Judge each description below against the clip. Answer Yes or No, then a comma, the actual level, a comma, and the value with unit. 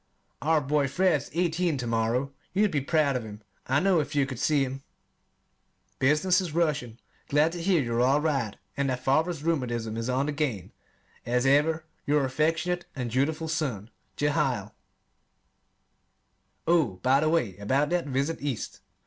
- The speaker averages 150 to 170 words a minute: Yes, average, 165 wpm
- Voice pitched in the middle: Yes, medium, 145 Hz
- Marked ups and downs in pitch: No, average, 4.0 semitones